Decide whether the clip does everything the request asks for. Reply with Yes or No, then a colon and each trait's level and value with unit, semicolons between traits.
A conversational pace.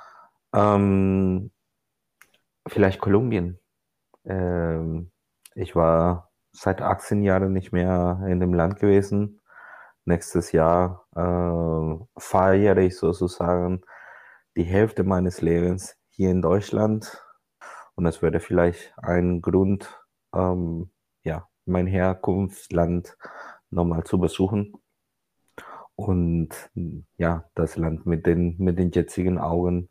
No: slow, 100 wpm